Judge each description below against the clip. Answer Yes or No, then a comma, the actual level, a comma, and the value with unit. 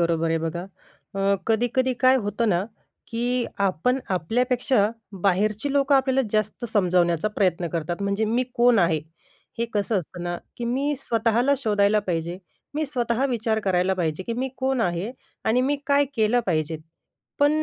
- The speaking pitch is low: No, high, 215 Hz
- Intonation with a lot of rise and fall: Yes, wide, 5.7 semitones